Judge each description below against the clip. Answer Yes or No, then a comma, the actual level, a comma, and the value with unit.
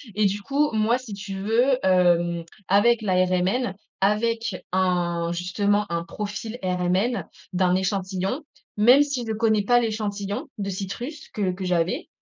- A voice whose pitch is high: Yes, high, 205 Hz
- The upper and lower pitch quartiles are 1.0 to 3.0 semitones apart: No, average, 3.8 semitones